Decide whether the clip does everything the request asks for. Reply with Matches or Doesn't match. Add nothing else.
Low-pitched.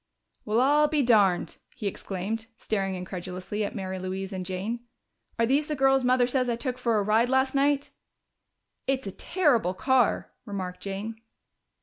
Doesn't match